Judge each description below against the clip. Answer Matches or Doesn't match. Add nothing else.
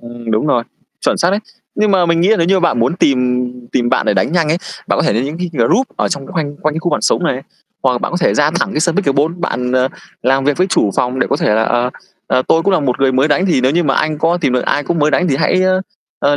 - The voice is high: Doesn't match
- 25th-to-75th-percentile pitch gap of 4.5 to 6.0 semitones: Matches